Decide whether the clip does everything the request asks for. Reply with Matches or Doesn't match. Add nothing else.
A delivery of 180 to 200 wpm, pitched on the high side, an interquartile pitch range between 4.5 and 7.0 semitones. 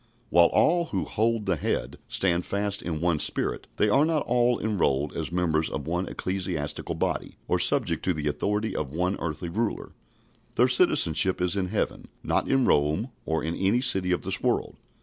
Doesn't match